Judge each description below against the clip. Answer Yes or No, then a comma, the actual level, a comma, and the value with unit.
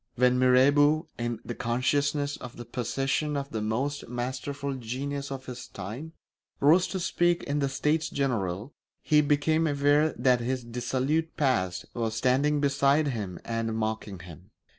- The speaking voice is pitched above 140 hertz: No, low, 130 Hz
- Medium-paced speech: Yes, average, 150 wpm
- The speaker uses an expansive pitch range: No, average, 3.5 semitones